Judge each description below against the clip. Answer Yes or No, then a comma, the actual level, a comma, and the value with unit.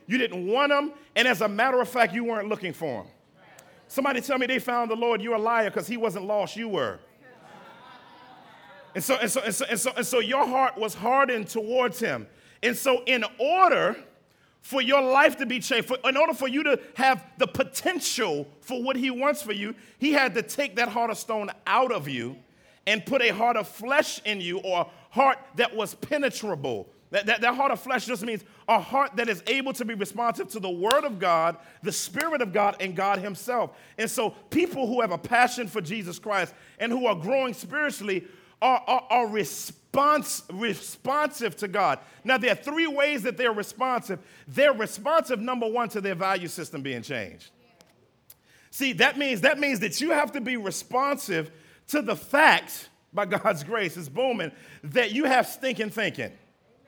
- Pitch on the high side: Yes, high, 235 Hz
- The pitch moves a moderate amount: Yes, average, 4.4 semitones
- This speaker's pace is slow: No, average, 200 wpm